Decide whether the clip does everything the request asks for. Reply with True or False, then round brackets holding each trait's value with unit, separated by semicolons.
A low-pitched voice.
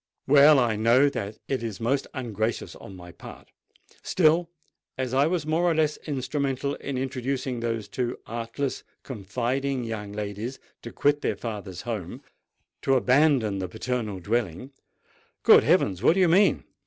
True (125 Hz)